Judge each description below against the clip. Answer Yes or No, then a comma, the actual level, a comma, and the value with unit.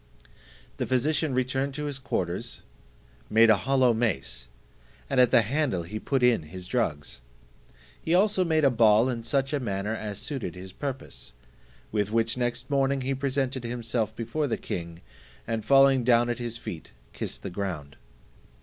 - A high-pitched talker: No, low, 120 Hz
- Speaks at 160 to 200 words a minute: Yes, average, 165 wpm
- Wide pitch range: No, average, 4.6 semitones